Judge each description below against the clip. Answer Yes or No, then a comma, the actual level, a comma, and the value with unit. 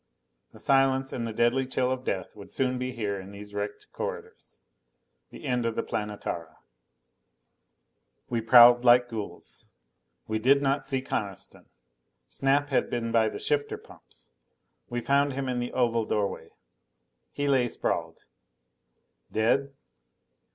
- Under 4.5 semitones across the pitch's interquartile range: Yes, average, 3.4 semitones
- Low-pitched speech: Yes, low, 120 Hz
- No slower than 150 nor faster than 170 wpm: No, average, 140 wpm